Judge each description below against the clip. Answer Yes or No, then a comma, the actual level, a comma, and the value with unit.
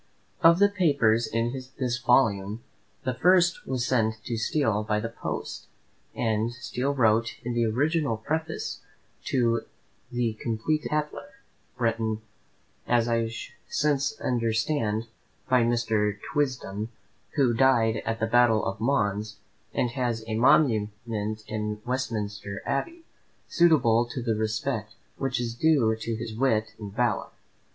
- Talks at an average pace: No, slow, 130 wpm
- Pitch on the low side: Yes, low, 115 Hz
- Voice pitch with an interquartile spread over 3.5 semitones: No, average, 3.2 semitones